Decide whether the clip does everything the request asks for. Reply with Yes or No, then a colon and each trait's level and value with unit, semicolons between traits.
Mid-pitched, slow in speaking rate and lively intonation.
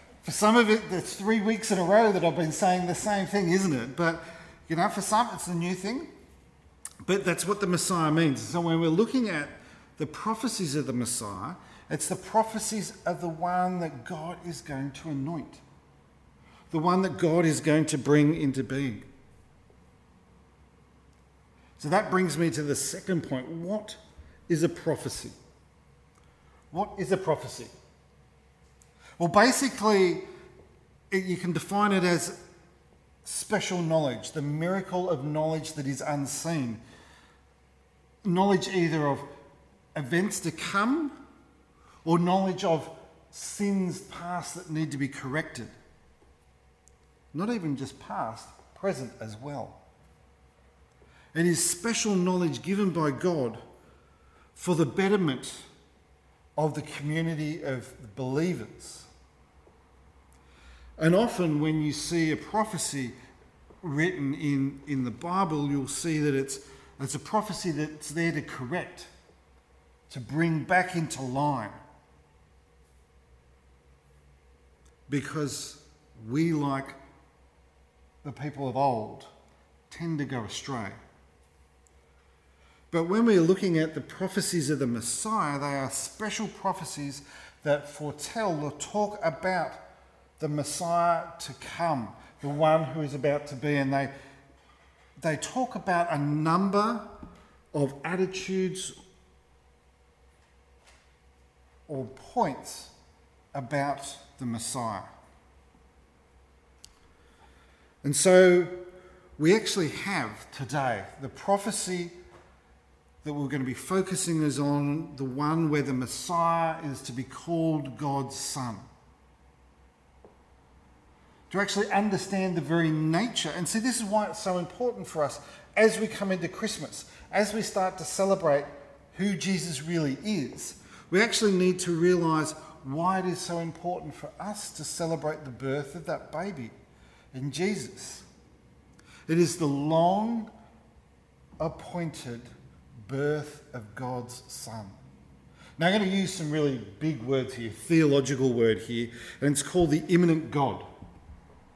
Yes: medium, 150 Hz; slow, 130 wpm; wide, 8.3 semitones